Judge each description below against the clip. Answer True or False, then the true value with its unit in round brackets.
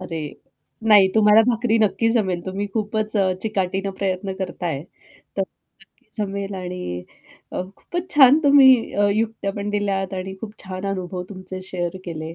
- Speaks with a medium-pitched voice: False (195 Hz)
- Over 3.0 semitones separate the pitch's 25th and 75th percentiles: False (2.5 semitones)